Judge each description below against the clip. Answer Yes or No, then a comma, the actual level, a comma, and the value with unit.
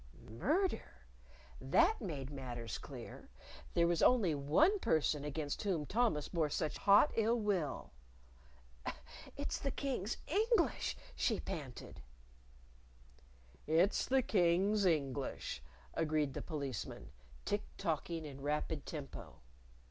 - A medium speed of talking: No, slow, 110 wpm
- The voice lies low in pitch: No, medium, 165 Hz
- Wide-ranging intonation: Yes, wide, 6.9 semitones